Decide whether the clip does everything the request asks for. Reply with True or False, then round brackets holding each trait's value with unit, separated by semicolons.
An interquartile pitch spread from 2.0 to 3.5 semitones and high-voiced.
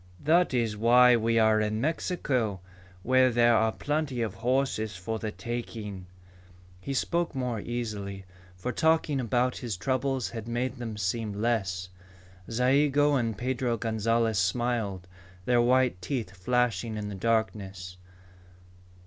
False (3.2 semitones; 115 Hz)